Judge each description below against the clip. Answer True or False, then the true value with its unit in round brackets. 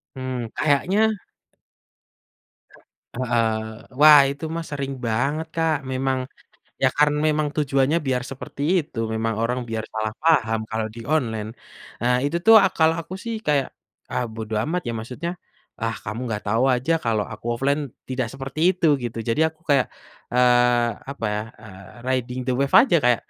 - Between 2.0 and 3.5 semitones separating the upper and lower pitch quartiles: False (4.8 semitones)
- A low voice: True (130 Hz)